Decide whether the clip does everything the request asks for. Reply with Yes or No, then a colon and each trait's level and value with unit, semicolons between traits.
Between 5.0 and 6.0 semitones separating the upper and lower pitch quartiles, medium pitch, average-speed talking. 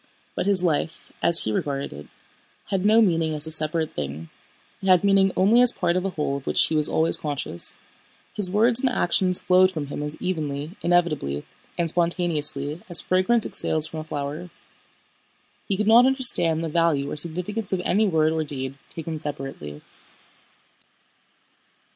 No: average, 4.0 semitones; medium, 165 Hz; average, 170 wpm